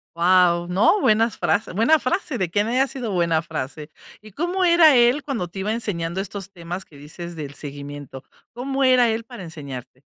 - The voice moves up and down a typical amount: No, wide, 6.6 semitones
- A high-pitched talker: Yes, high, 195 Hz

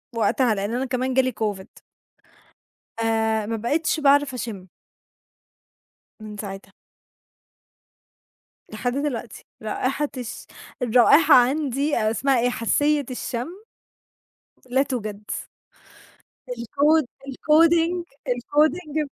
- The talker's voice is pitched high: Yes, very high, 250 Hz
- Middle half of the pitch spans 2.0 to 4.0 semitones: No, average, 4.6 semitones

